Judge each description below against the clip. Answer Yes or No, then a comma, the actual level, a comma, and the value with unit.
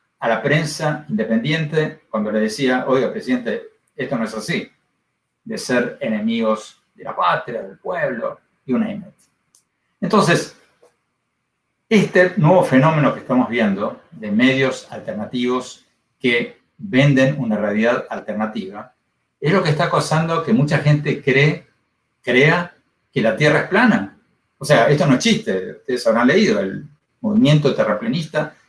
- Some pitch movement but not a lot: No, wide, 6.2 semitones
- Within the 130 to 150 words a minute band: Yes, average, 140 wpm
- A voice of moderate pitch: Yes, medium, 145 Hz